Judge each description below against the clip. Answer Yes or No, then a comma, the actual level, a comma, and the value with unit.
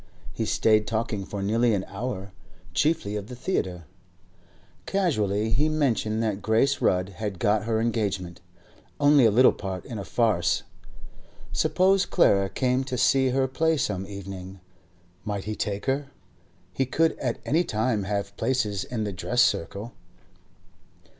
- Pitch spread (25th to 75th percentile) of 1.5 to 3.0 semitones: No, average, 4.5 semitones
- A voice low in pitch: Yes, low, 110 Hz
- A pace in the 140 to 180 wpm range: Yes, average, 145 wpm